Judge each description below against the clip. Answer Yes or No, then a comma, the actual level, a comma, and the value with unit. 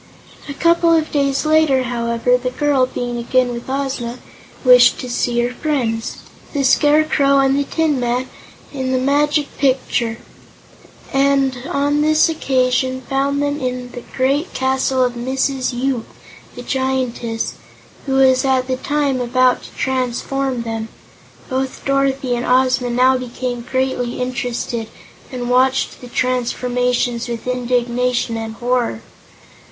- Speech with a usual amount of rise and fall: No, narrow, 1.8 semitones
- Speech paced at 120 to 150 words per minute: Yes, slow, 135 wpm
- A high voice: Yes, very high, 255 Hz